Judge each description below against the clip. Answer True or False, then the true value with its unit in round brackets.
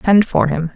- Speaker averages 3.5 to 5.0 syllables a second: True (4.7 syllables/s)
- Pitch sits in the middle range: True (175 Hz)